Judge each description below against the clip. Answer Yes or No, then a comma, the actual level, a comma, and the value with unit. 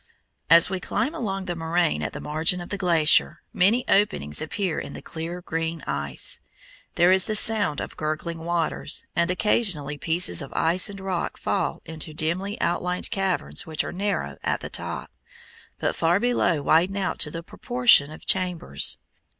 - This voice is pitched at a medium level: Yes, medium, 175 Hz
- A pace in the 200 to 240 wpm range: No, average, 170 wpm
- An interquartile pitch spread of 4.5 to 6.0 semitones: No, average, 3.3 semitones